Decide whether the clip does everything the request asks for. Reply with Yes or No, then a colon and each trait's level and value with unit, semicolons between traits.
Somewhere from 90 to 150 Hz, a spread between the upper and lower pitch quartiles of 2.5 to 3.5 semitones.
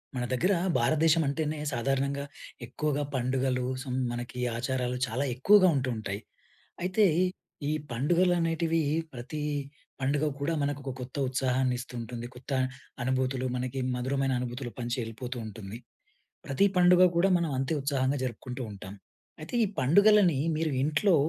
No: low, 135 Hz; average, 3.9 semitones